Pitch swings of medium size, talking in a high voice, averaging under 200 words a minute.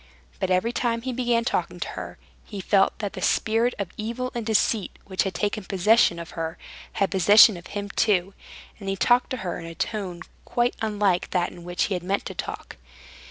No: average, 3.7 semitones; high, 205 Hz; fast, 205 wpm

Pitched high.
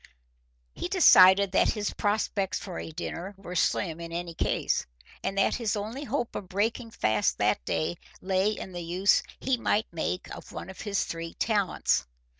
Yes: high, 195 Hz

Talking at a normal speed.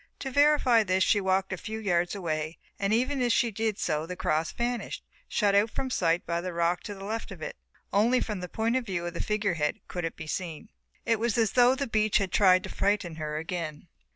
No: fast, 235 wpm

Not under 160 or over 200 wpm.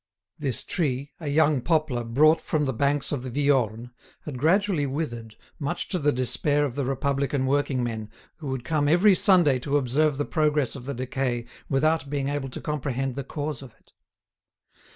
Yes: average, 180 wpm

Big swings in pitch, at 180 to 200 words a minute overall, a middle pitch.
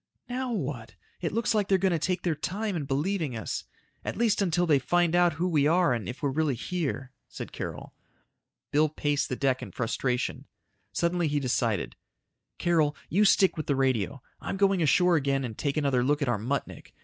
No: average, 4.8 semitones; average, 195 wpm; medium, 155 Hz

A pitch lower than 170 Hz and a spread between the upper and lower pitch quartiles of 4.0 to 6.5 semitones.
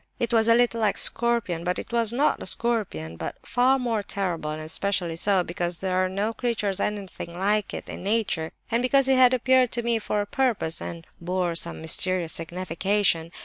No: high, 200 Hz; average, 5.3 semitones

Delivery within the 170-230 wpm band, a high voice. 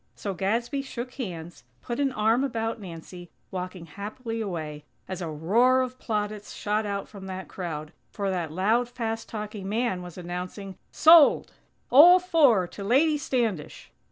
No: average, 155 wpm; high, 210 Hz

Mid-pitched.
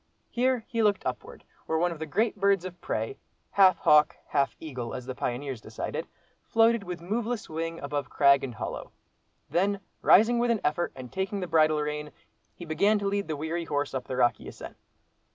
Yes: medium, 165 Hz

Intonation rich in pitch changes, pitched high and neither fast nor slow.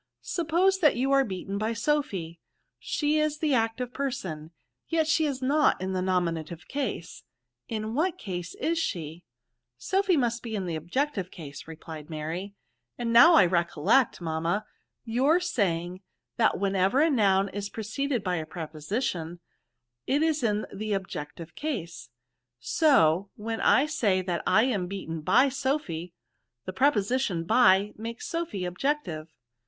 Yes: wide, 8.0 semitones; high, 205 Hz; average, 155 wpm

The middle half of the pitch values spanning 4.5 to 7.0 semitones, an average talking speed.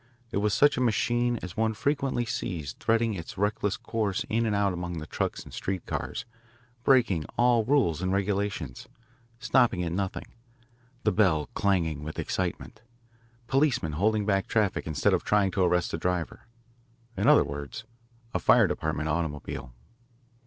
Yes: average, 4.9 semitones; average, 155 wpm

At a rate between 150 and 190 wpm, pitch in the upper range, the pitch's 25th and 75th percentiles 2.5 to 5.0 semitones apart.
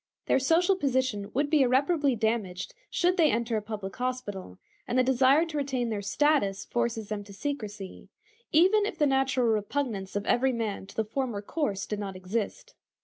No: average, 180 wpm; high, 240 Hz; wide, 5.5 semitones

